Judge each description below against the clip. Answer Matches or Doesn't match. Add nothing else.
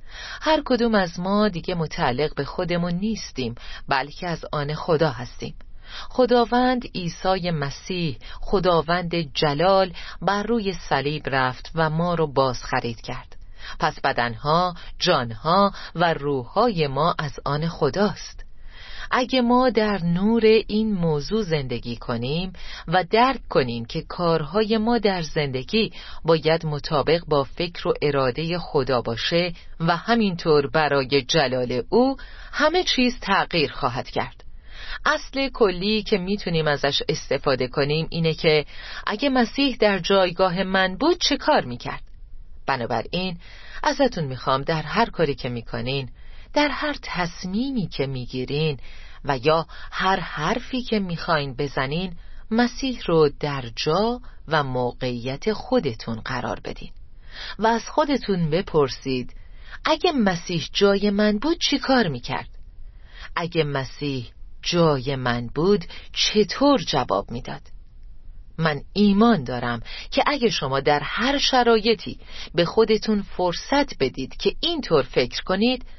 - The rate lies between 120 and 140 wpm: Matches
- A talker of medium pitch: Matches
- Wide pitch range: Matches